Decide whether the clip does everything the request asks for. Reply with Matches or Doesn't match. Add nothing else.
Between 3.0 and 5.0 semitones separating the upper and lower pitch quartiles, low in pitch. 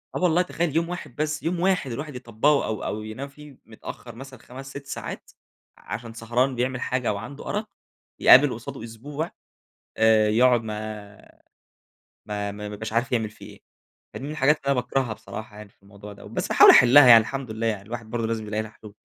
Matches